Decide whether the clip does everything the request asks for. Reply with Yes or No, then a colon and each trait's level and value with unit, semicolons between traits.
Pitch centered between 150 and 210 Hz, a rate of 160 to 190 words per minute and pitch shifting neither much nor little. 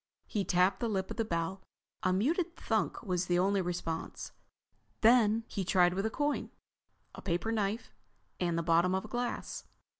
Yes: high, 190 Hz; average, 175 wpm; average, 3.9 semitones